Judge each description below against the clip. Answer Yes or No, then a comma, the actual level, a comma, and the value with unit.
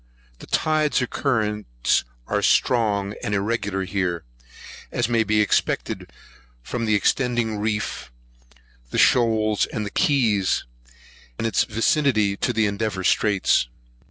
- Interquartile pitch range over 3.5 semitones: No, narrow, 2.6 semitones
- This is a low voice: Yes, low, 110 Hz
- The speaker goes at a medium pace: No, slow, 110 wpm